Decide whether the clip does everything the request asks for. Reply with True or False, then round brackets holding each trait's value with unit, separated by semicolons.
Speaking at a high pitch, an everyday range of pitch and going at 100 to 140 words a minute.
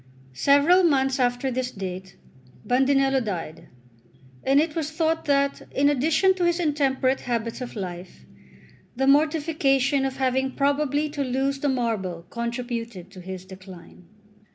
True (265 Hz; 3.8 semitones; 135 wpm)